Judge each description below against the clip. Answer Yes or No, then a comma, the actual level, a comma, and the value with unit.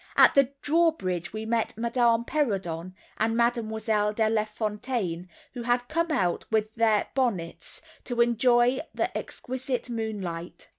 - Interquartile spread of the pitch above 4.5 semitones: No, average, 2.7 semitones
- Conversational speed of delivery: No, slow, 130 wpm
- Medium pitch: No, high, 225 Hz